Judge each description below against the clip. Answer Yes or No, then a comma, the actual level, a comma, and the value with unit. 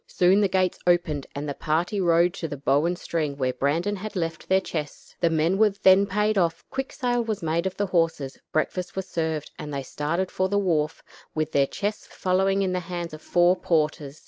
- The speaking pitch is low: No, medium, 175 Hz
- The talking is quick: Yes, fast, 215 wpm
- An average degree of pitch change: Yes, average, 3.6 semitones